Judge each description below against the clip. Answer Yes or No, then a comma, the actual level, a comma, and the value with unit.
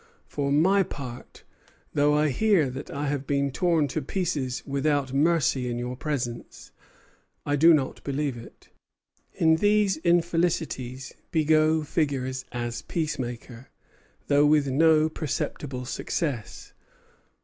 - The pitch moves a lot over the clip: No, average, 3.5 semitones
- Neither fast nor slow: No, slow, 120 wpm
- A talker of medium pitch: Yes, medium, 145 Hz